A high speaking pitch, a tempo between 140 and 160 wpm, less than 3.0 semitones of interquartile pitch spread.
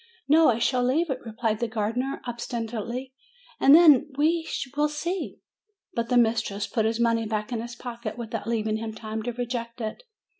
No: high, 235 Hz; average, 185 wpm; narrow, 2.5 semitones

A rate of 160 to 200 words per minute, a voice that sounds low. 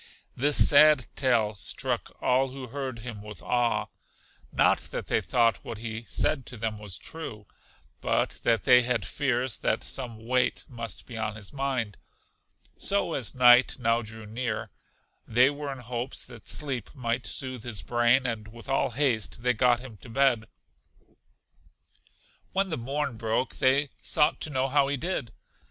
Yes: average, 165 wpm; low, 125 Hz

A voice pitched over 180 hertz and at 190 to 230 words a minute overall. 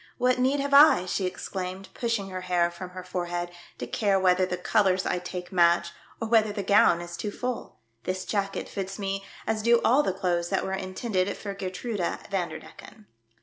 Yes: high, 190 Hz; average, 200 wpm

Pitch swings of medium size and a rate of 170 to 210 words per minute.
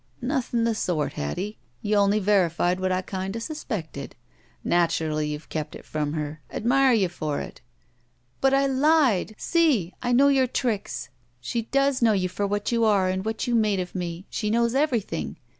No: wide, 5.7 semitones; average, 175 wpm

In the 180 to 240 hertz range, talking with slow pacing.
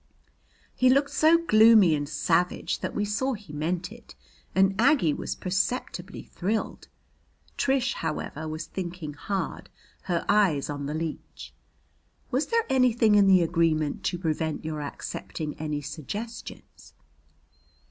Yes: medium, 185 Hz; slow, 130 wpm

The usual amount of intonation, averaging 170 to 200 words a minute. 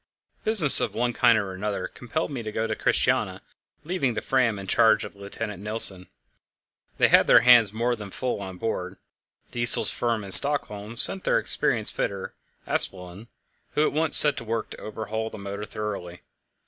Yes: average, 3.3 semitones; average, 175 wpm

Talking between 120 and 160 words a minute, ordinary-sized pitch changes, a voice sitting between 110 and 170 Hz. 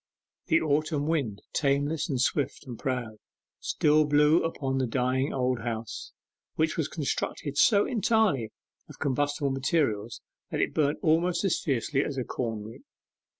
Yes: average, 150 wpm; average, 3.6 semitones; medium, 140 Hz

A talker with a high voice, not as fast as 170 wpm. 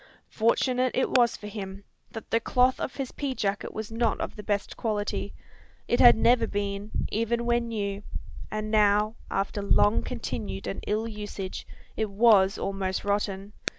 Yes: high, 210 Hz; average, 160 wpm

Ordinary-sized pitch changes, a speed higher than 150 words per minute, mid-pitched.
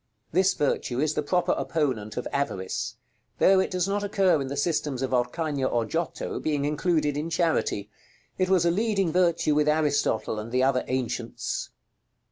Yes: average, 5.0 semitones; average, 170 wpm; medium, 150 Hz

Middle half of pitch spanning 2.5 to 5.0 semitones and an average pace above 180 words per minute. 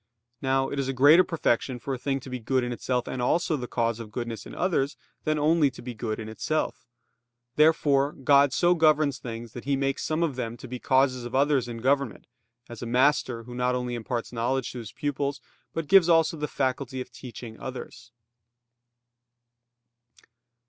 Yes: average, 2.9 semitones; average, 190 wpm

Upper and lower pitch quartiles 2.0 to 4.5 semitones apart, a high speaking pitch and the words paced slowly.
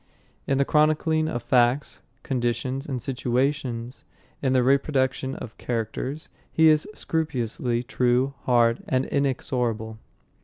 No: narrow, 2.5 semitones; low, 130 Hz; slow, 115 wpm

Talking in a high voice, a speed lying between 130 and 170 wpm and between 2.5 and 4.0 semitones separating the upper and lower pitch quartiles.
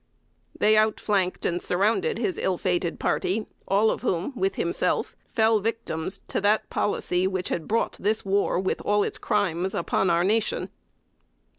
Yes: high, 200 Hz; average, 160 wpm; average, 3.1 semitones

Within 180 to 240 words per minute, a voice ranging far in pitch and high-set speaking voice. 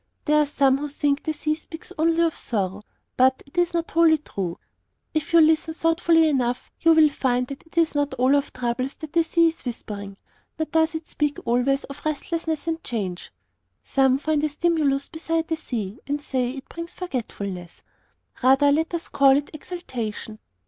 No: average, 190 wpm; average, 4.0 semitones; very high, 290 Hz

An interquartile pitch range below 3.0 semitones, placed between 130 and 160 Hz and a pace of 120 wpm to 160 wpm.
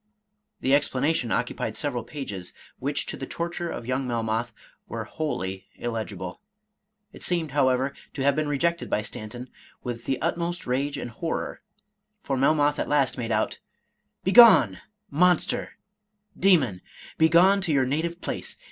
No: average, 5.3 semitones; low, 135 Hz; average, 150 wpm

